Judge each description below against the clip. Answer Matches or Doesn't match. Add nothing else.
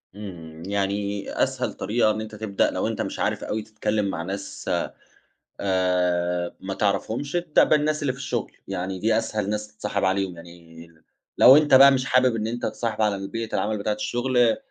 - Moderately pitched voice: Doesn't match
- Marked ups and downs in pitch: Doesn't match